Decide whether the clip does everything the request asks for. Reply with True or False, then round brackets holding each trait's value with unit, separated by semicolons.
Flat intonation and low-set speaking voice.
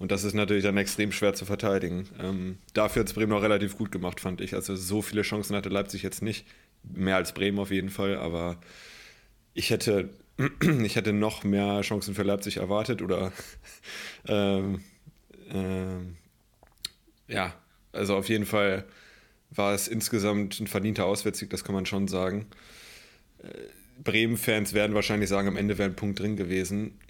True (1.6 semitones; 100 Hz)